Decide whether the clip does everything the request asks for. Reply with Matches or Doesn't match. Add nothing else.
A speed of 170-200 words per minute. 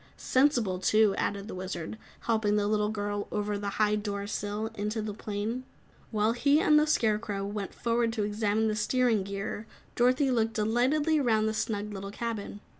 Matches